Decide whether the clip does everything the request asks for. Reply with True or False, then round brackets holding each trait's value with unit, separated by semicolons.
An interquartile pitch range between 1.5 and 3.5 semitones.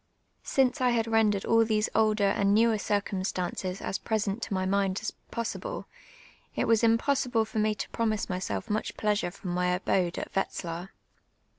True (2.8 semitones)